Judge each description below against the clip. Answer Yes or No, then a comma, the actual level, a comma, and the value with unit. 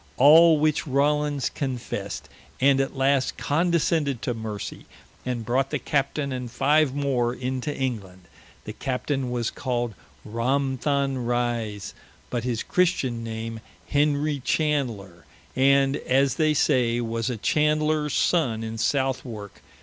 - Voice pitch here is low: Yes, low, 130 Hz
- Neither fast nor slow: No, slow, 125 wpm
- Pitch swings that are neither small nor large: Yes, average, 3.4 semitones